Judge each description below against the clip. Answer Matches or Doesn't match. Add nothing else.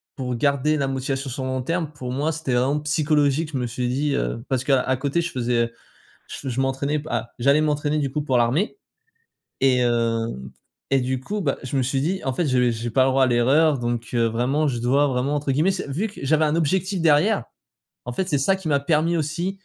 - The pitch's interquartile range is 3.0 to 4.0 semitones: Matches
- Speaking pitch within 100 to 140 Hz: Matches